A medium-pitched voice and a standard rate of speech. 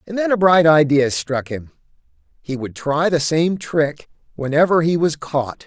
Yes: medium, 155 Hz; average, 180 wpm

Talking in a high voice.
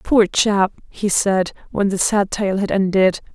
Yes: high, 195 Hz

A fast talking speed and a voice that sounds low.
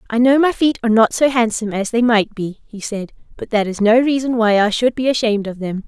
No: fast, 265 wpm; high, 230 Hz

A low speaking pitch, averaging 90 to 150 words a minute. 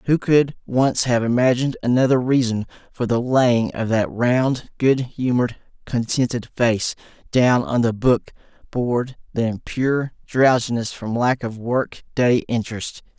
Yes: low, 120 Hz; average, 140 wpm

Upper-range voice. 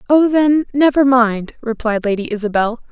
Yes: high, 245 Hz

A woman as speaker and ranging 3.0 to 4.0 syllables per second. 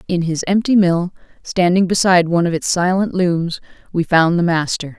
No: female; 5.5 syllables/s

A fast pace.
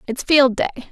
No: average, 195 wpm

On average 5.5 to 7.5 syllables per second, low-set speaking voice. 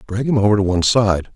Yes: 6.7 syllables/s; low, 105 Hz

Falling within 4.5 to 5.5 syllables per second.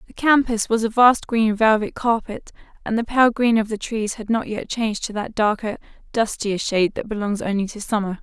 Yes: 5.3 syllables/s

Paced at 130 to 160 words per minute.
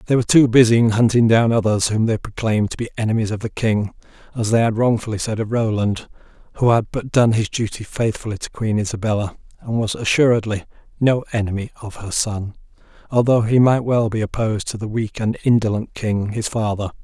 No: average, 195 wpm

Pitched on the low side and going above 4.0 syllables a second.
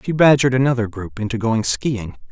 Yes: low, 120 Hz; 5.8 syllables/s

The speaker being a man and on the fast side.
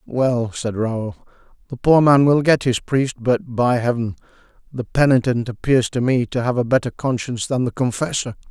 No: male; average, 185 wpm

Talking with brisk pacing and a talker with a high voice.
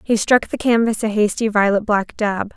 Yes: fast, 210 wpm; high, 215 Hz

